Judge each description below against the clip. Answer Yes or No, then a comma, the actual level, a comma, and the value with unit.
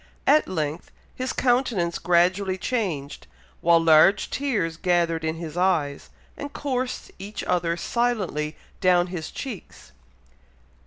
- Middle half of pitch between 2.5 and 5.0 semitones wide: No, wide, 5.5 semitones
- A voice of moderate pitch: Yes, medium, 180 Hz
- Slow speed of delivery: Yes, slow, 115 wpm